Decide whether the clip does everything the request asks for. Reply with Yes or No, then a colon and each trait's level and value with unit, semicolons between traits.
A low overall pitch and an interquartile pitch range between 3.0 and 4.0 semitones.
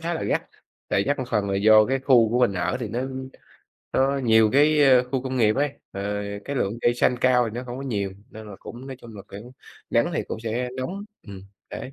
Yes: low, 120 Hz; average, 3.6 semitones